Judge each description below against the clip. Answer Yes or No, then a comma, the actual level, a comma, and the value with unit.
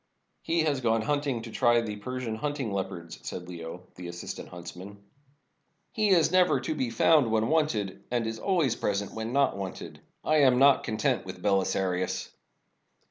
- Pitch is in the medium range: No, low, 115 Hz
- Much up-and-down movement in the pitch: Yes, wide, 6.4 semitones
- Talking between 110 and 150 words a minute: No, average, 170 wpm